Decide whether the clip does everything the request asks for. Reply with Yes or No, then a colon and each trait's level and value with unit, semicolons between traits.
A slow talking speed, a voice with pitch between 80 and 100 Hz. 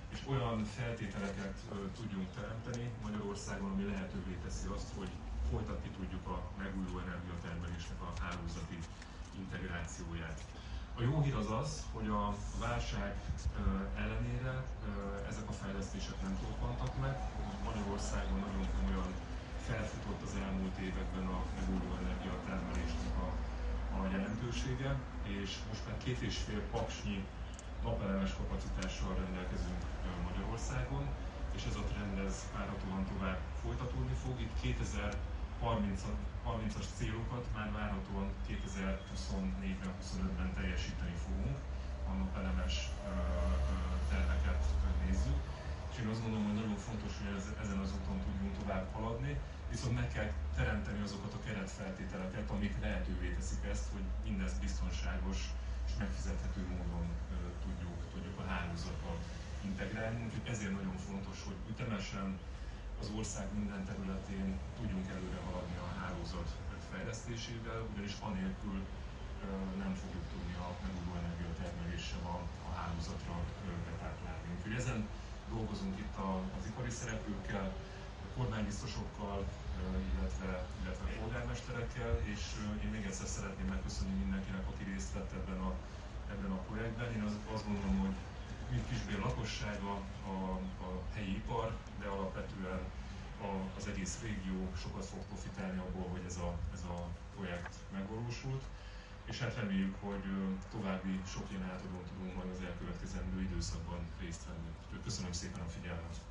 No: average, 120 wpm; very low, 95 Hz